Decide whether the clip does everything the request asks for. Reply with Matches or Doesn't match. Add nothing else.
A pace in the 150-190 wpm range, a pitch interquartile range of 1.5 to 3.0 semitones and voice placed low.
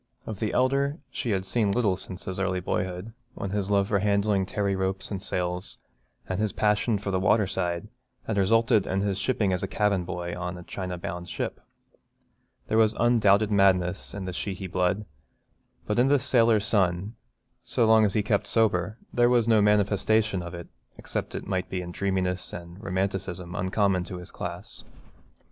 Matches